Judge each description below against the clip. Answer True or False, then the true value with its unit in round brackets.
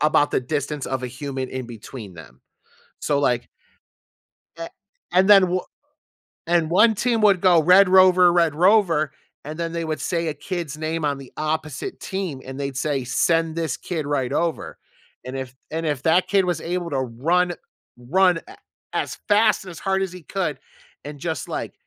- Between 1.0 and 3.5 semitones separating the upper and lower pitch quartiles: False (4.6 semitones)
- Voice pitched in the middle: True (160 Hz)